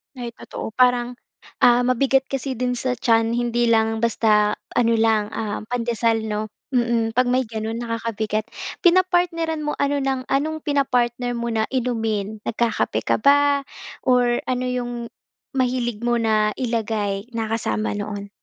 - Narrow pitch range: Yes, narrow, 2.3 semitones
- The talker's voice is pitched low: No, high, 240 Hz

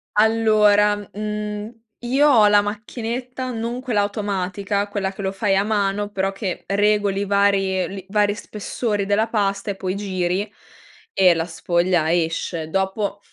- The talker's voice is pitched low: No, high, 205 Hz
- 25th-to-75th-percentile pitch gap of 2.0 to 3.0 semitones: No, narrow, 1.6 semitones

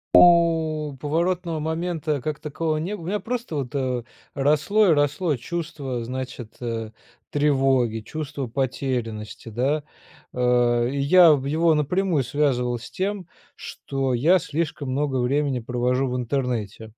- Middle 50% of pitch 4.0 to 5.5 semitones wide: Yes, average, 4.4 semitones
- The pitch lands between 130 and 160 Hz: Yes, medium, 140 Hz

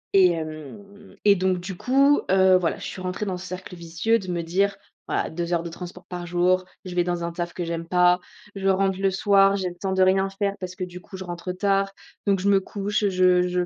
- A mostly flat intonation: Yes, narrow, 1.7 semitones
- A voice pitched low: No, medium, 185 Hz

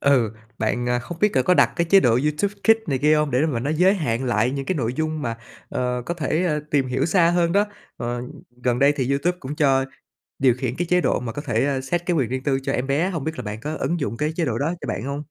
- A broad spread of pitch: No, average, 4.9 semitones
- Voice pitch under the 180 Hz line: Yes, medium, 140 Hz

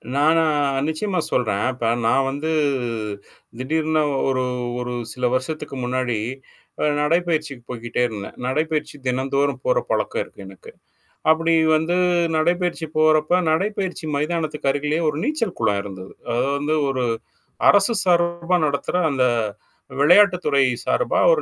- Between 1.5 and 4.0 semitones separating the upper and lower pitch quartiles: No, average, 4.7 semitones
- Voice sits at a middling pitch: Yes, medium, 155 Hz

